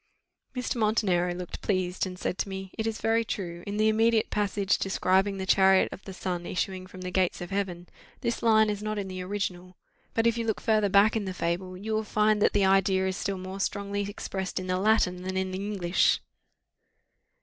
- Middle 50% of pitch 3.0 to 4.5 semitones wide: No, narrow, 2.4 semitones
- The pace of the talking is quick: Yes, fast, 215 wpm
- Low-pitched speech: No, high, 195 Hz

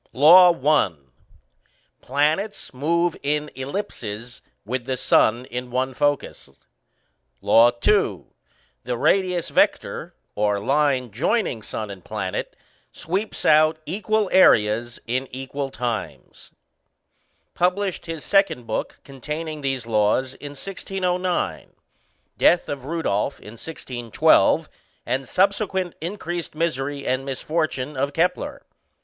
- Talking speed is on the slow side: Yes, slow, 105 wpm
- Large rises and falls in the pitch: Yes, wide, 5.7 semitones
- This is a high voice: No, medium, 145 Hz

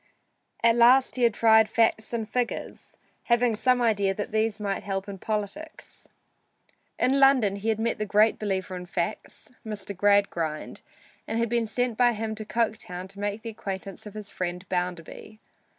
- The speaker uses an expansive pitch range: No, average, 2.8 semitones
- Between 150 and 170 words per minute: Yes, average, 165 wpm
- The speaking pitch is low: No, high, 215 Hz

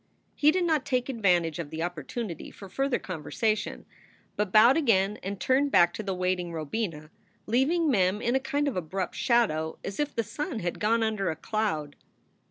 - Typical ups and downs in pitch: No, wide, 6.1 semitones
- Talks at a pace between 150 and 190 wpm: Yes, average, 180 wpm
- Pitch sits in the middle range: No, high, 210 Hz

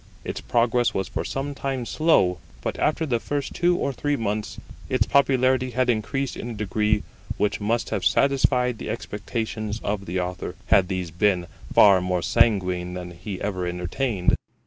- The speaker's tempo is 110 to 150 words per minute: No, average, 170 wpm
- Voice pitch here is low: Yes, low, 110 Hz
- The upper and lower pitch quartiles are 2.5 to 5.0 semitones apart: No, wide, 5.6 semitones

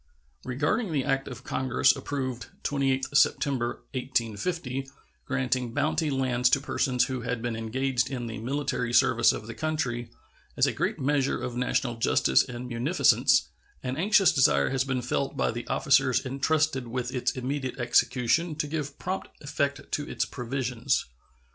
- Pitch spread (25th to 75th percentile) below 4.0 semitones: Yes, narrow, 2.6 semitones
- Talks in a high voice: No, low, 130 Hz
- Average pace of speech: Yes, average, 155 wpm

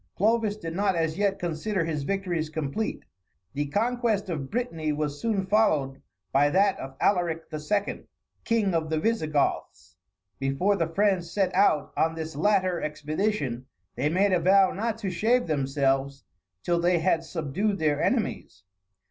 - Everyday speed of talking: Yes, average, 150 wpm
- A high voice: No, medium, 170 Hz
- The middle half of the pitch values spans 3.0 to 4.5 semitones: No, average, 4.9 semitones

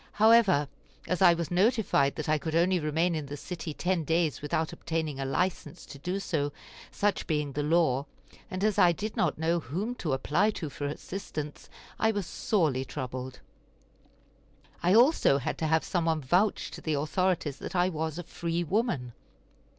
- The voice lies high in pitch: No, medium, 165 Hz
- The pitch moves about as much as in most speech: Yes, average, 3.9 semitones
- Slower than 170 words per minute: No, average, 180 wpm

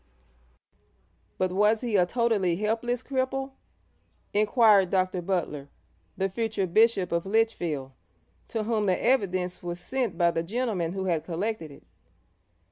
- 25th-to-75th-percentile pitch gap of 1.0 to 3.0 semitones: No, average, 4.2 semitones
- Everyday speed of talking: No, slow, 130 wpm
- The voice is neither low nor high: No, high, 195 Hz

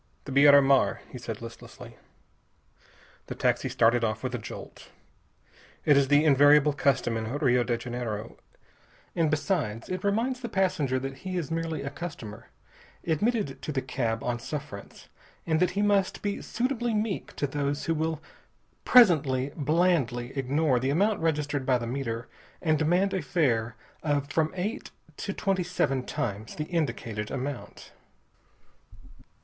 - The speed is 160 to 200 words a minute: No, average, 150 wpm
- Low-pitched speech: No, medium, 145 Hz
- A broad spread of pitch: Yes, wide, 5.7 semitones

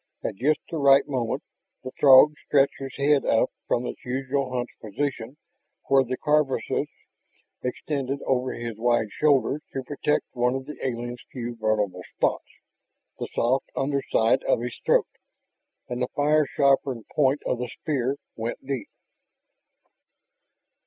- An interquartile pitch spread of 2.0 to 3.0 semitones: Yes, narrow, 2.5 semitones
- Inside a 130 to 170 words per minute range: Yes, average, 140 wpm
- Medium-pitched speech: No, low, 130 Hz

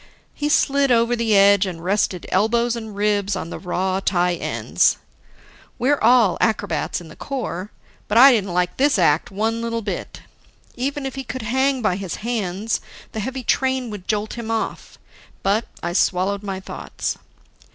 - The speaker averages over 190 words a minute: No, average, 170 wpm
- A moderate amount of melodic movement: Yes, average, 4.1 semitones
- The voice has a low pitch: No, high, 215 Hz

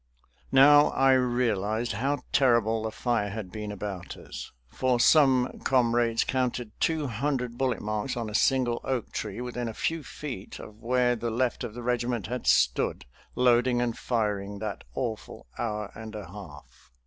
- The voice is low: Yes, low, 120 Hz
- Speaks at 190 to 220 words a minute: No, average, 160 wpm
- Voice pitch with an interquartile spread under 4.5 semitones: Yes, average, 2.9 semitones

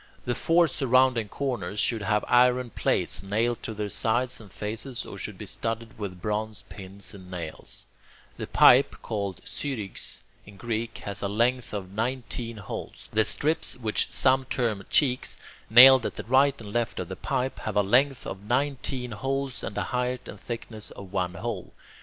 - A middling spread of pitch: Yes, average, 3.6 semitones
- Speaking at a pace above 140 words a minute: Yes, average, 175 wpm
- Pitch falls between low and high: No, low, 115 Hz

